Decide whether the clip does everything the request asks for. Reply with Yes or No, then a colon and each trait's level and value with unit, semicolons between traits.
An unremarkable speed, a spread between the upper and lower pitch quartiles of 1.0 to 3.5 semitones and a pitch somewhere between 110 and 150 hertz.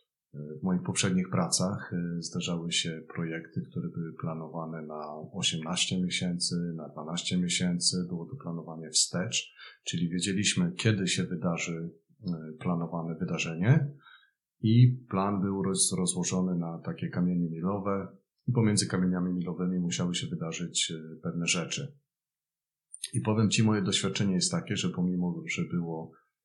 No: average, 125 wpm; average, 2.9 semitones; very low, 90 Hz